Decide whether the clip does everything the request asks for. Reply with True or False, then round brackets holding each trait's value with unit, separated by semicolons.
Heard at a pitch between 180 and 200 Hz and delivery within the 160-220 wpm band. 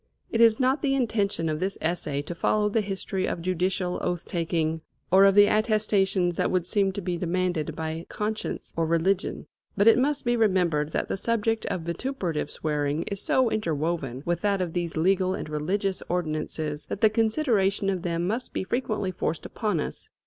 True (185 Hz; 185 wpm)